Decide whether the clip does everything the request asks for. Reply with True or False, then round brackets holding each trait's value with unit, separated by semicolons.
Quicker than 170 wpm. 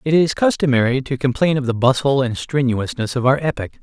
True (205 wpm)